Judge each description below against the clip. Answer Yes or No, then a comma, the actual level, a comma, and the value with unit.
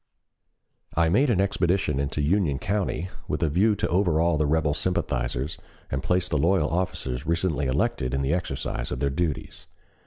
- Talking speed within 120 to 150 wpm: No, average, 165 wpm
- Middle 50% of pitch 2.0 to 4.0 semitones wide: No, average, 4.5 semitones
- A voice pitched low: Yes, very low, 80 Hz